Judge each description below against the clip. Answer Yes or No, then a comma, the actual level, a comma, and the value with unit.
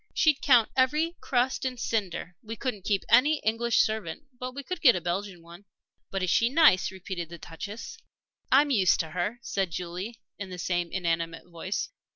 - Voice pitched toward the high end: Yes, high, 205 Hz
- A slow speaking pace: No, average, 185 wpm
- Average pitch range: No, wide, 6.1 semitones